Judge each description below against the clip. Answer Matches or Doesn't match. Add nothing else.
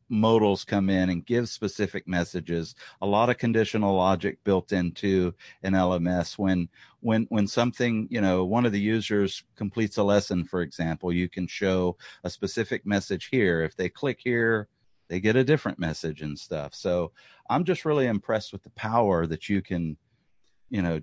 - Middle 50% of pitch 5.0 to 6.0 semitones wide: Doesn't match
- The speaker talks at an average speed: Matches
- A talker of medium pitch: Doesn't match